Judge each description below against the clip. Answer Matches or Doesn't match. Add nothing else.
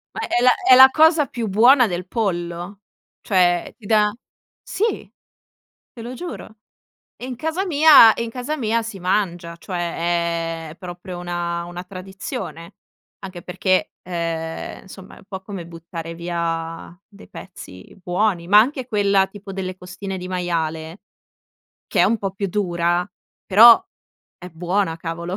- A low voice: Doesn't match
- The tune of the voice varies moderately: Matches